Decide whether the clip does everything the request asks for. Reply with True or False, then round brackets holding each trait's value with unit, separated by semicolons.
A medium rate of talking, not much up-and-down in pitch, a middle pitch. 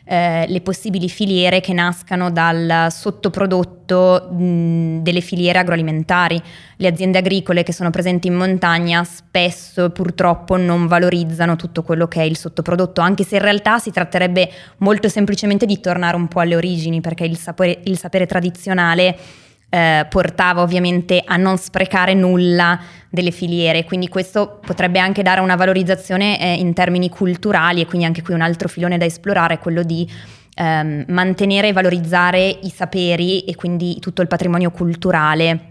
True (160 wpm; 1.5 semitones; 180 Hz)